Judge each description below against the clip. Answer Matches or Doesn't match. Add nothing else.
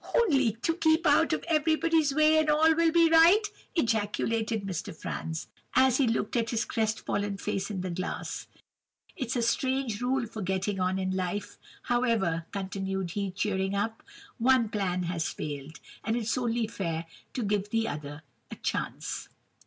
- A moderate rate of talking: Matches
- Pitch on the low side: Doesn't match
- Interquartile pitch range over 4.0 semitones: Matches